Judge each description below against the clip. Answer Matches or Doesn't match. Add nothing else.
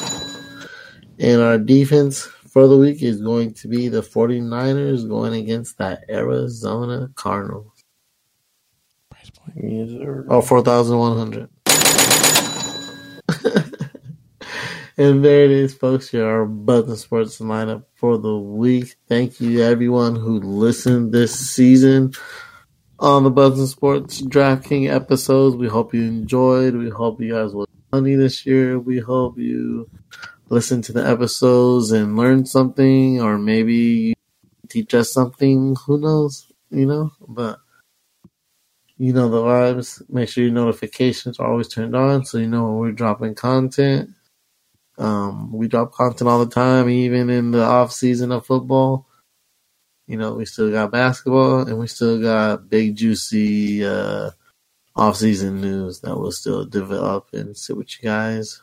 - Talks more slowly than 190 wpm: Matches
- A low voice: Matches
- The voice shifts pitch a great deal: Doesn't match